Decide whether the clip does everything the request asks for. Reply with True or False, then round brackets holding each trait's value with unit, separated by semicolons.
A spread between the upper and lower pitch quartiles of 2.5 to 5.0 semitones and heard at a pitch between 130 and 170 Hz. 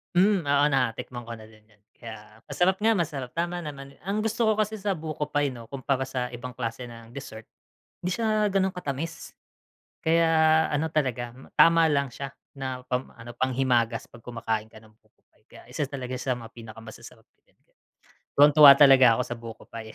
False (5.4 semitones; 135 Hz)